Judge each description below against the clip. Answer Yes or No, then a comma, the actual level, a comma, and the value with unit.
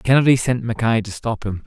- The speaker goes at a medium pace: No, fast, 215 wpm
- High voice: No, low, 115 Hz